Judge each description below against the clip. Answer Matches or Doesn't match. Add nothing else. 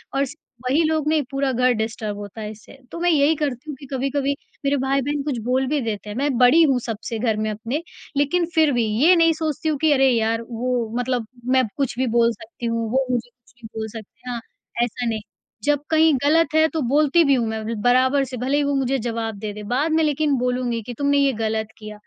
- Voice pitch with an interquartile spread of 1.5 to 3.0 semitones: Doesn't match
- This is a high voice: Matches